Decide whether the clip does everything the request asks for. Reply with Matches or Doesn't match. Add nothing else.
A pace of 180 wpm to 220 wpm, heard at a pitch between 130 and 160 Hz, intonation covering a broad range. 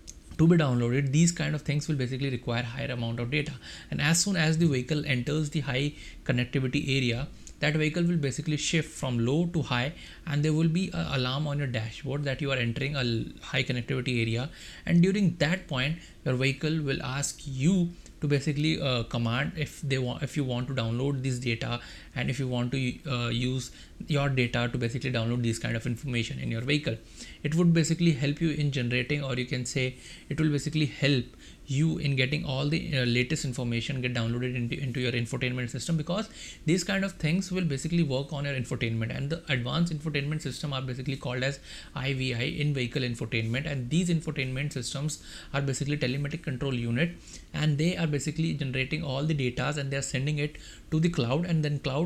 Doesn't match